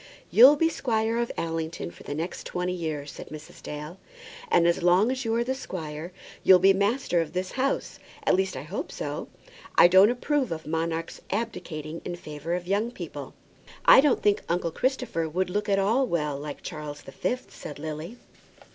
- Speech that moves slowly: No, average, 190 wpm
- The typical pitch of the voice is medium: Yes, medium, 180 Hz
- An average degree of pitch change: No, wide, 6.1 semitones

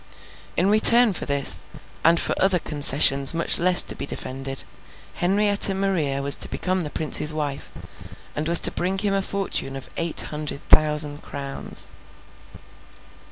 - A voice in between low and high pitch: Yes, medium, 155 Hz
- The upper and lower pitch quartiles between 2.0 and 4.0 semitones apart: No, average, 5.1 semitones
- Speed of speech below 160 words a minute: Yes, average, 150 wpm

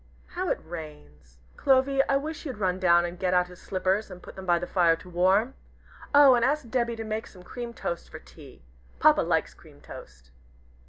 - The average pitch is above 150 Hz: Yes, medium, 185 Hz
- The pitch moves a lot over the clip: Yes, wide, 6.0 semitones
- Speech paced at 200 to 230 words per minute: Yes, fast, 205 wpm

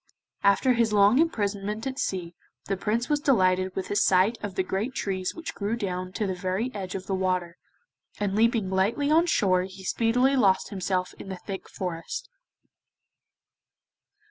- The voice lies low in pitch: No, high, 200 Hz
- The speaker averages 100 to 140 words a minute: No, average, 170 wpm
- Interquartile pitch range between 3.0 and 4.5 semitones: Yes, average, 3.6 semitones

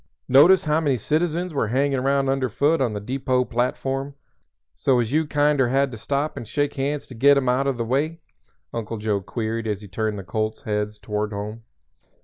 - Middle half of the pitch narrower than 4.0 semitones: No, average, 4.4 semitones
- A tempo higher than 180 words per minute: Yes, average, 195 wpm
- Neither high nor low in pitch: No, low, 130 Hz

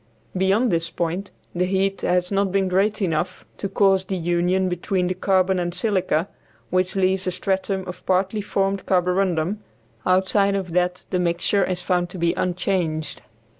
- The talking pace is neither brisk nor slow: Yes, average, 165 wpm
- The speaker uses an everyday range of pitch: No, narrow, 1.5 semitones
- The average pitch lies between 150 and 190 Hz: Yes, medium, 185 Hz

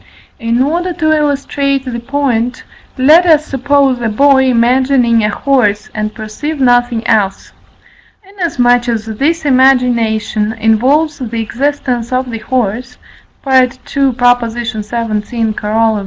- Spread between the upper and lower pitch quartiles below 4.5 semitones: Yes, average, 3.5 semitones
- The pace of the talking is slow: Yes, slow, 115 wpm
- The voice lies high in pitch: Yes, high, 245 Hz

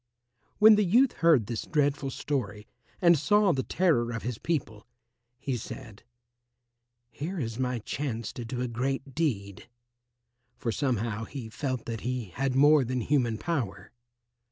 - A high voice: No, low, 130 Hz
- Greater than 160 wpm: No, average, 150 wpm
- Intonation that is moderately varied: Yes, average, 4.4 semitones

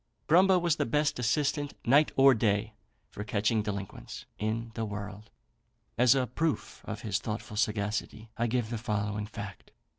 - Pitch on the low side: Yes, low, 110 Hz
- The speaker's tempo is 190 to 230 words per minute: No, average, 155 wpm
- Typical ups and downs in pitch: Yes, average, 3.9 semitones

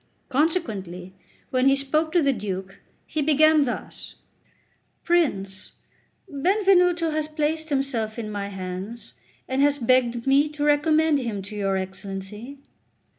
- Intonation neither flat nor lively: No, wide, 7.2 semitones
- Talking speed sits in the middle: No, slow, 125 wpm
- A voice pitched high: Yes, very high, 270 Hz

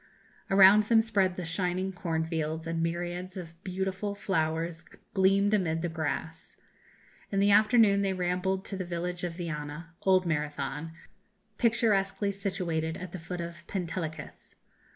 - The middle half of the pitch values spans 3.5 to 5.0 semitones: No, average, 3.0 semitones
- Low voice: No, medium, 180 Hz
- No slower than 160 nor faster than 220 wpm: No, average, 140 wpm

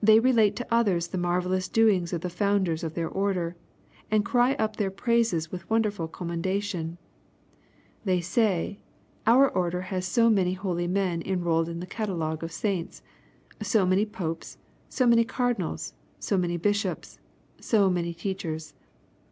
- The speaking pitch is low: No, medium, 185 Hz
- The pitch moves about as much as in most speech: Yes, average, 3.9 semitones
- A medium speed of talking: Yes, average, 150 wpm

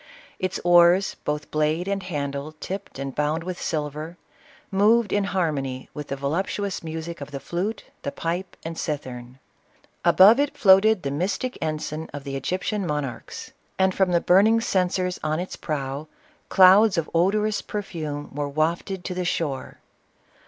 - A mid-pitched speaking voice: Yes, medium, 170 Hz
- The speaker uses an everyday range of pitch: Yes, average, 4.4 semitones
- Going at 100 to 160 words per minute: Yes, average, 155 wpm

